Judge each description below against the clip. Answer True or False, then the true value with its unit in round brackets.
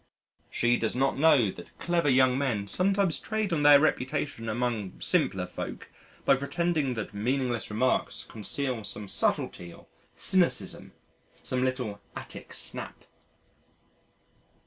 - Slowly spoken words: True (125 wpm)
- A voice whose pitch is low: True (130 Hz)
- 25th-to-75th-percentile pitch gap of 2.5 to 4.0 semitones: False (4.8 semitones)